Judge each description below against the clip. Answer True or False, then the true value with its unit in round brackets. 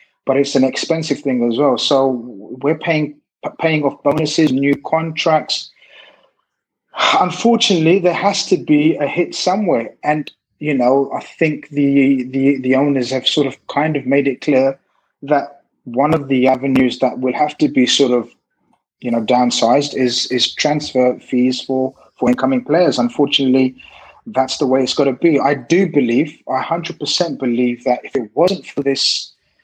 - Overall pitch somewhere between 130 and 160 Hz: True (140 Hz)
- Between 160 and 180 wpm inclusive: True (170 wpm)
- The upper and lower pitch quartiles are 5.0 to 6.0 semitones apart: False (2.7 semitones)